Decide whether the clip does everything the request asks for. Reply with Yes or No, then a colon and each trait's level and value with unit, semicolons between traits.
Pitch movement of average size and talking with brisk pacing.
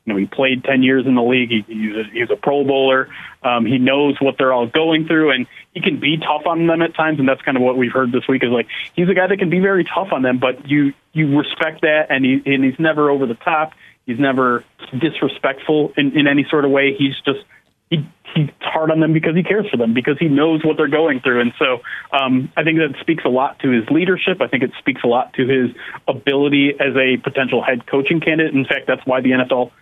Yes: average, 3.5 semitones; fast, 260 wpm